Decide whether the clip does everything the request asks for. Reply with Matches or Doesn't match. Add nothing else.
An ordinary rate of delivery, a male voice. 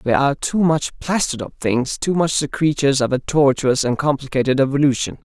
Matches